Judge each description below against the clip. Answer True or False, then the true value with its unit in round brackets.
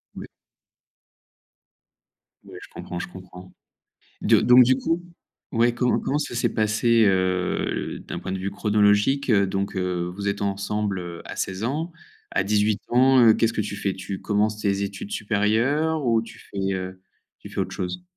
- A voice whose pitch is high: False (105 Hz)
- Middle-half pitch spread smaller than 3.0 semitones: False (3.6 semitones)